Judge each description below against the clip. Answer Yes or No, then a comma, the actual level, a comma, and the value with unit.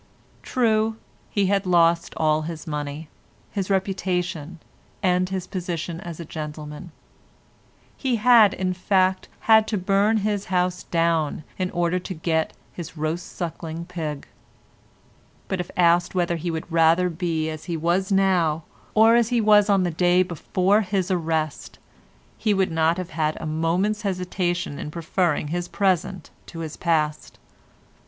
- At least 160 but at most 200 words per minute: No, average, 150 wpm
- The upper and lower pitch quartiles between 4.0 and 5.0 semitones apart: No, average, 2.8 semitones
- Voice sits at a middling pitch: Yes, medium, 175 Hz